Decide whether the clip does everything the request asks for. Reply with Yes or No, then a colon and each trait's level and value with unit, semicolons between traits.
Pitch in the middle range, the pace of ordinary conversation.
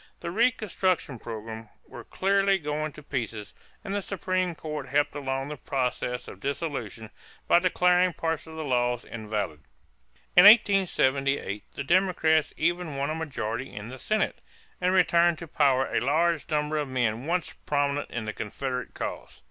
Yes: medium, 150 Hz; average, 155 wpm